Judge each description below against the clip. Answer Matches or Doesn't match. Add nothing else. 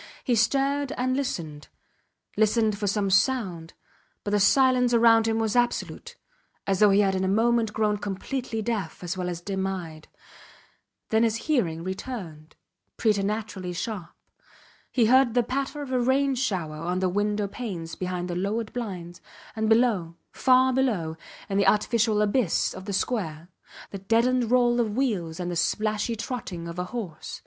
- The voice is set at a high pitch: Matches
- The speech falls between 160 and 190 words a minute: Matches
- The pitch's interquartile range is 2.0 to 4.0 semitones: Doesn't match